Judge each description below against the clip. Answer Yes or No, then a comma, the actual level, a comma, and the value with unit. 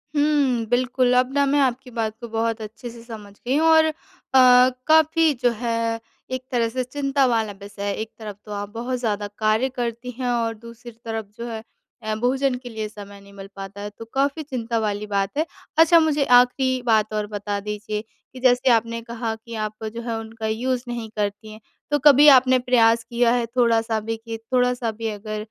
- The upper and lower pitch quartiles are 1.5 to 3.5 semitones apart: Yes, average, 2.7 semitones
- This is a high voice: Yes, high, 235 Hz